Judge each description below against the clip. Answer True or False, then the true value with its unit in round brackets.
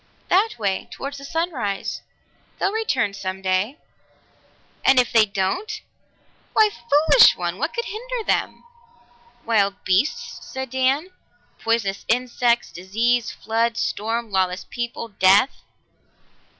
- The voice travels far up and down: True (5.7 semitones)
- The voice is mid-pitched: False (235 Hz)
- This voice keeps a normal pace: False (115 wpm)